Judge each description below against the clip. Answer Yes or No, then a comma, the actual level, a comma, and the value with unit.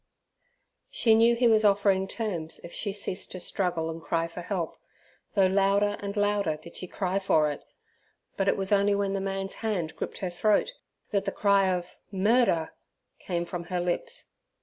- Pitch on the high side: Yes, high, 195 Hz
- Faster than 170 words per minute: Yes, average, 180 wpm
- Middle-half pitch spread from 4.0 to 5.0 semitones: No, average, 2.7 semitones